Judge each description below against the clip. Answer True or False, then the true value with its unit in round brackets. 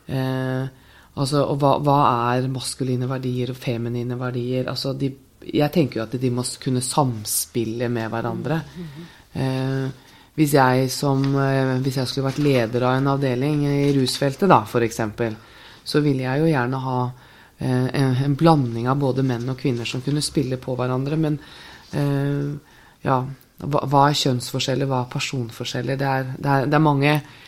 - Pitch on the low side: True (130 Hz)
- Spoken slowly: False (160 wpm)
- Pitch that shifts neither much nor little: False (2.0 semitones)